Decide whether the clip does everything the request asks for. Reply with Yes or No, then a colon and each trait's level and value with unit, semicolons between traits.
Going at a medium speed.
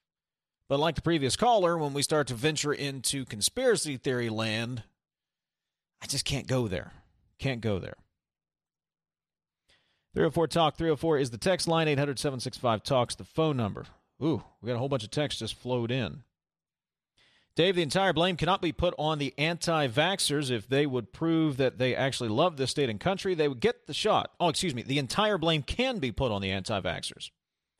Yes: average, 180 wpm